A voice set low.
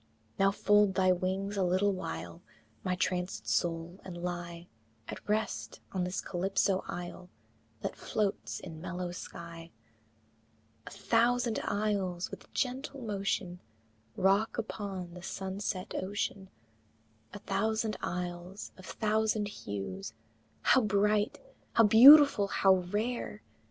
No: high, 195 Hz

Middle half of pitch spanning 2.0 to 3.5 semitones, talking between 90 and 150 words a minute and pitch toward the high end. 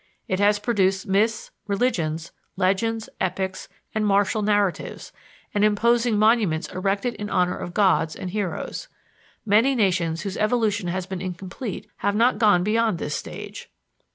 Yes: average, 2.8 semitones; average, 140 wpm; high, 205 Hz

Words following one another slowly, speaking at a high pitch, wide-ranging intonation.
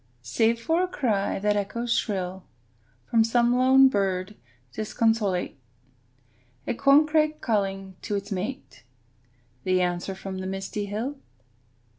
No: slow, 120 wpm; high, 210 Hz; average, 4.1 semitones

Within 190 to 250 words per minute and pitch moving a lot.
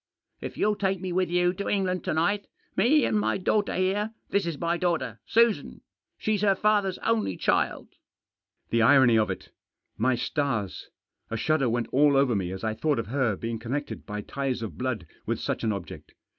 Yes: average, 200 wpm; wide, 8.8 semitones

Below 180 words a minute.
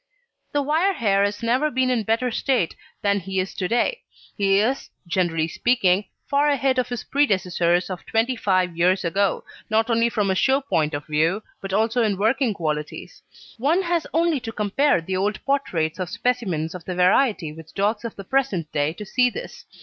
No: average, 190 wpm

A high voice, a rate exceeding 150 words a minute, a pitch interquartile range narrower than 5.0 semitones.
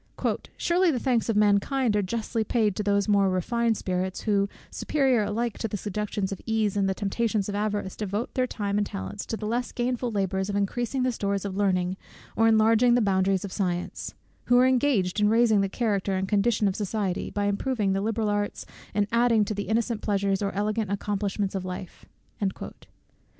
Yes: high, 205 Hz; average, 190 wpm; narrow, 2.5 semitones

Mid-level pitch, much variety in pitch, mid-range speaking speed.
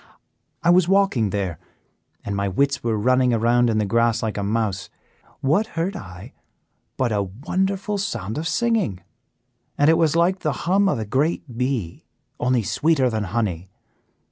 No: low, 120 Hz; wide, 7.9 semitones; average, 165 wpm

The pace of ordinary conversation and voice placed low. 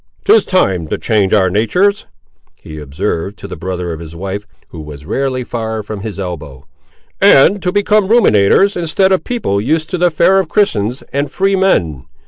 Yes: average, 180 wpm; low, 110 Hz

